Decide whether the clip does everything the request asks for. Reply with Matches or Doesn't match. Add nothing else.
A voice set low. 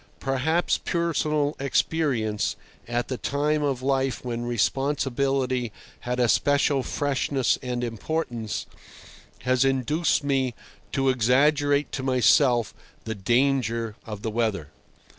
Matches